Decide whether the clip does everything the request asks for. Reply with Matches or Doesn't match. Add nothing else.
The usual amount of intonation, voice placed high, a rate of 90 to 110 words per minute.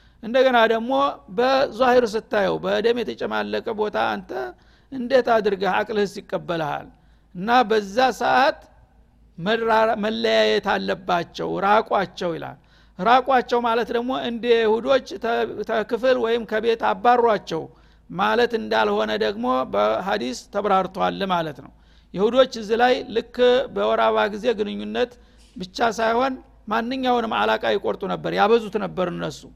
Matches